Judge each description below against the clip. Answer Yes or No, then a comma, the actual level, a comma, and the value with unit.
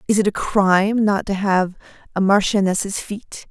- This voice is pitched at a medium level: No, high, 200 Hz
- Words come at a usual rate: Yes, average, 170 wpm